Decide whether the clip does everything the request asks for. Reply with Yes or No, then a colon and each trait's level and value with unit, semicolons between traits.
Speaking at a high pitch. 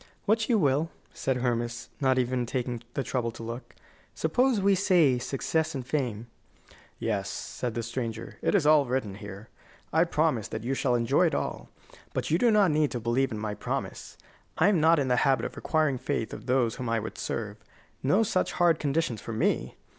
No: low, 130 Hz